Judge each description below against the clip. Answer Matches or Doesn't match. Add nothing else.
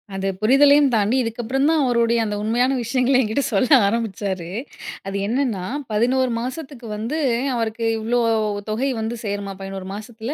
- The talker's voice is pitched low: Doesn't match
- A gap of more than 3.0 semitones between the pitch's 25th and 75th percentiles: Matches